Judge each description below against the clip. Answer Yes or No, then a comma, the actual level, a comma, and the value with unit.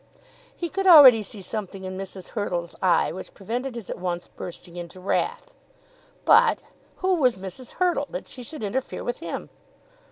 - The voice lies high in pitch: Yes, high, 215 Hz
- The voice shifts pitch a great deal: Yes, wide, 6.5 semitones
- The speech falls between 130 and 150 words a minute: No, average, 165 wpm